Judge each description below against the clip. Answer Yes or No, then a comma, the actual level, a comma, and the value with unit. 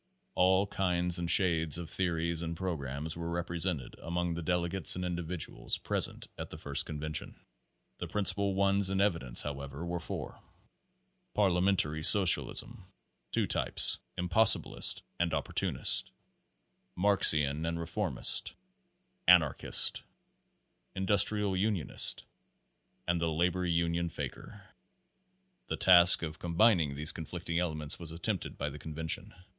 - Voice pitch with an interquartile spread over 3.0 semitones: No, narrow, 2.6 semitones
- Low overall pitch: Yes, very low, 85 Hz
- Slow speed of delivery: Yes, slow, 125 wpm